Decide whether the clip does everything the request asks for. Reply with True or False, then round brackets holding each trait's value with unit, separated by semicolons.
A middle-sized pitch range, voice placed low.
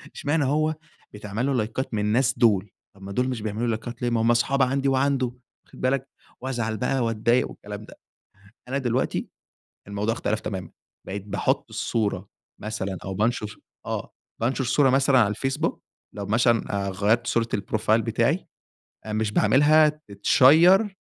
True (4.1 semitones; 115 Hz)